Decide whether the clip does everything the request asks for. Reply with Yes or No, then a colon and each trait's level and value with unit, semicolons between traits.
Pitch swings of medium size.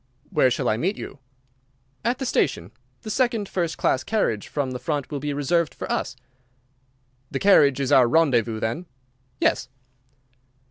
No: wide, 6.1 semitones